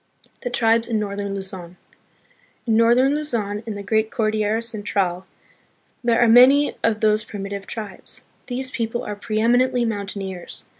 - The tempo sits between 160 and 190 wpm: No, average, 145 wpm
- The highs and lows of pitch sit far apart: No, average, 2.8 semitones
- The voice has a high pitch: Yes, high, 220 Hz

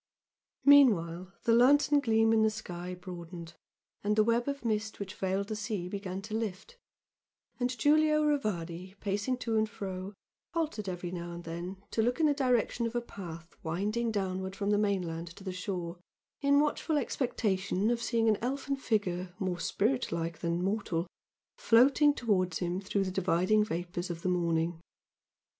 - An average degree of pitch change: Yes, average, 4.7 semitones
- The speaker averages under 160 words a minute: No, average, 165 wpm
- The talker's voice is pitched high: Yes, high, 200 Hz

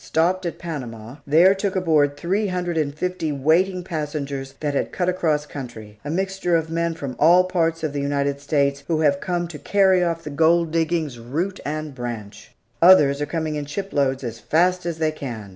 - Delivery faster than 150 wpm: Yes, average, 195 wpm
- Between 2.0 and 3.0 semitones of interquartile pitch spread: No, average, 3.7 semitones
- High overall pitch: No, medium, 155 Hz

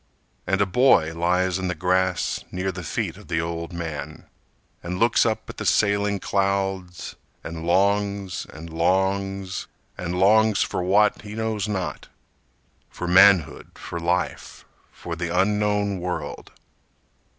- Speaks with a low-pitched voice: Yes, very low, 95 Hz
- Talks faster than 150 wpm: No, average, 140 wpm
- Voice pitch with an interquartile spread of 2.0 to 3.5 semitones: Yes, narrow, 2.5 semitones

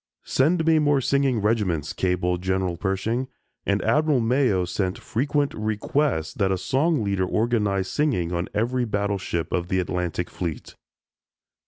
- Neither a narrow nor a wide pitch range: No, wide, 6.2 semitones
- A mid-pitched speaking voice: No, low, 105 Hz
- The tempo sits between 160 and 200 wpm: No, average, 140 wpm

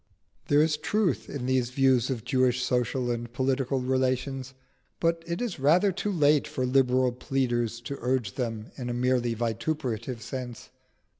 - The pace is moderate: Yes, average, 155 wpm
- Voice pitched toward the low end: Yes, low, 130 Hz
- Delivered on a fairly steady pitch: Yes, narrow, 2.3 semitones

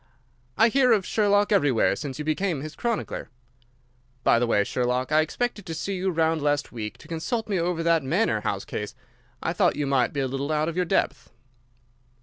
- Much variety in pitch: Yes, wide, 6.1 semitones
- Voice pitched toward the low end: No, medium, 160 Hz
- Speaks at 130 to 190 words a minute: No, average, 200 wpm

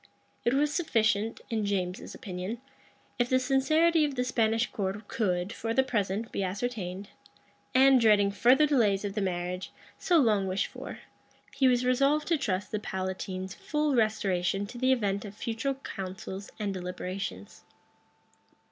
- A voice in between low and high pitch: No, high, 215 Hz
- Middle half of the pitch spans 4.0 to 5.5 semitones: Yes, average, 5.1 semitones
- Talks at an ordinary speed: Yes, average, 150 wpm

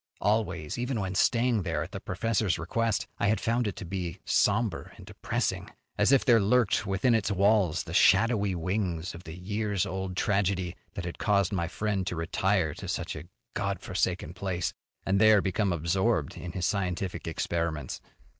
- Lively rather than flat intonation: No, average, 3.5 semitones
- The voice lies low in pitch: Yes, very low, 95 Hz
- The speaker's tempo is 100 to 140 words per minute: No, average, 175 wpm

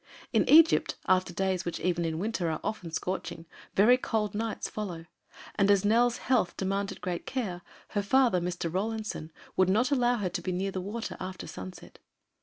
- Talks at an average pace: Yes, average, 180 wpm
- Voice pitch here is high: Yes, high, 195 Hz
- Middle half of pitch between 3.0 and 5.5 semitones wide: Yes, average, 3.9 semitones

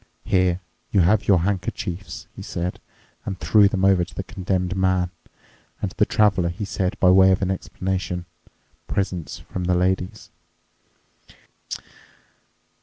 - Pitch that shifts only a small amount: Yes, narrow, 1.2 semitones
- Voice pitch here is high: No, very low, 95 Hz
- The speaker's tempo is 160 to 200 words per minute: No, average, 140 wpm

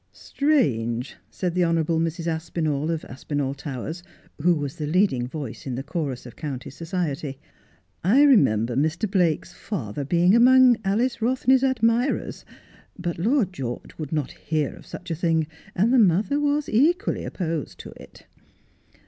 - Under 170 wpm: Yes, average, 150 wpm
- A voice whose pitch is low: No, medium, 165 Hz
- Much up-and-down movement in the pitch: Yes, wide, 7.4 semitones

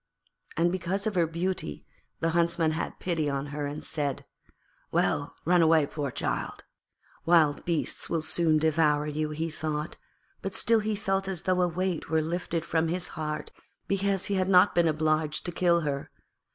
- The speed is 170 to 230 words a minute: Yes, average, 175 wpm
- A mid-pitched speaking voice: Yes, medium, 165 Hz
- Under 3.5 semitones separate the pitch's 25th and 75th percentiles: Yes, average, 2.8 semitones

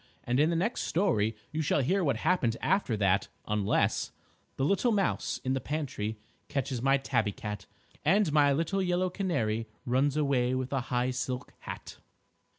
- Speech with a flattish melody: No, wide, 5.5 semitones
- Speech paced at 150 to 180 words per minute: Yes, average, 165 wpm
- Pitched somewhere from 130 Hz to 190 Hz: Yes, low, 135 Hz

